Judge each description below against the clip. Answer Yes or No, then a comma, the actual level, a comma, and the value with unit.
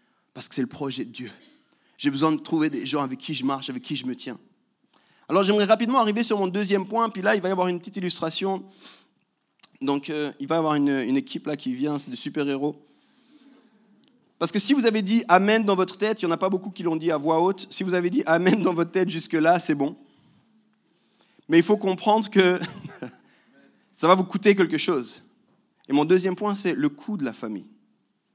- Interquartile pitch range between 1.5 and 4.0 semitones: No, average, 5.1 semitones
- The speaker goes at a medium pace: No, fast, 230 wpm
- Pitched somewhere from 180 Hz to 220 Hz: Yes, medium, 185 Hz